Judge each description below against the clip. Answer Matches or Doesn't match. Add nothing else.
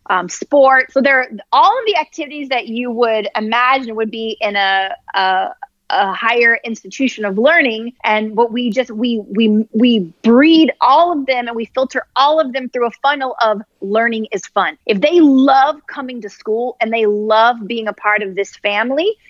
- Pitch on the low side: Doesn't match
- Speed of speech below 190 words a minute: Doesn't match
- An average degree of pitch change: Matches